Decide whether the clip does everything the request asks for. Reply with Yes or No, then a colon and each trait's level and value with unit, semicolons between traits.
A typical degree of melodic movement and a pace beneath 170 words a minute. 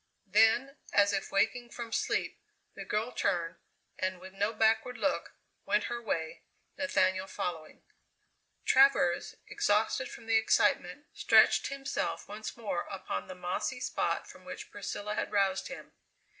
Yes: average, 4.0 semitones; average, 140 wpm